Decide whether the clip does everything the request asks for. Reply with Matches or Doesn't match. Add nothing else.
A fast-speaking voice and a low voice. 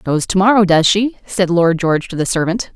Doesn't match